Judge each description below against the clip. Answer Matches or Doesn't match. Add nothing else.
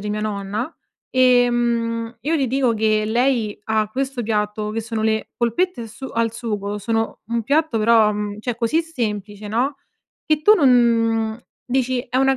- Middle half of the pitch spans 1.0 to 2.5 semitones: Doesn't match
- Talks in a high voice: Matches